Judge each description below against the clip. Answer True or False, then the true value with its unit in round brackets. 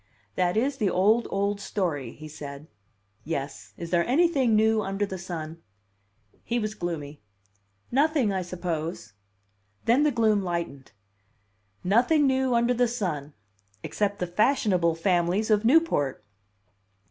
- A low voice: False (195 Hz)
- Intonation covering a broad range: True (5.8 semitones)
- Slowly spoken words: True (130 wpm)